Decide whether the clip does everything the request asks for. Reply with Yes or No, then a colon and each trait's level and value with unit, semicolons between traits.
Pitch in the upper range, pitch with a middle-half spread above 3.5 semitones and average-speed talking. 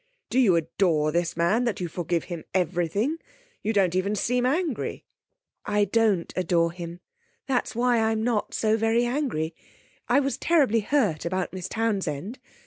Yes: high, 205 Hz; wide, 5.6 semitones; average, 160 wpm